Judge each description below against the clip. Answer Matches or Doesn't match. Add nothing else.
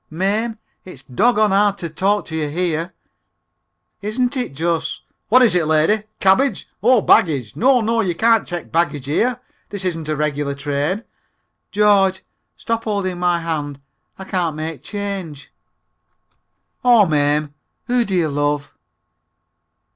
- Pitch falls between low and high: Matches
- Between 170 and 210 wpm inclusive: Doesn't match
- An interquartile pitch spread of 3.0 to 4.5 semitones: Doesn't match